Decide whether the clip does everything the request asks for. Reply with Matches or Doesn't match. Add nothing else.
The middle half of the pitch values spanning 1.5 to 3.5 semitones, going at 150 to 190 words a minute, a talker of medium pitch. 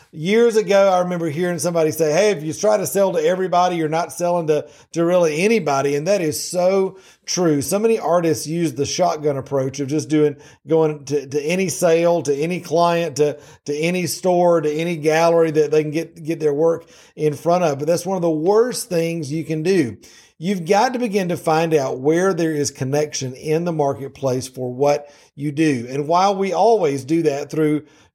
Doesn't match